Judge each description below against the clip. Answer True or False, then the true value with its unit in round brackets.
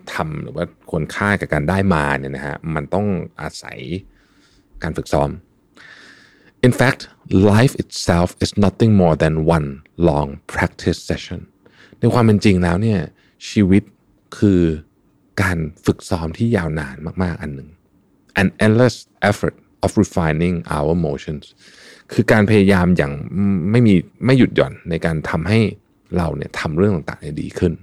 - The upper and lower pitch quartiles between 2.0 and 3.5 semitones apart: False (4.4 semitones)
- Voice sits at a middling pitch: False (95 Hz)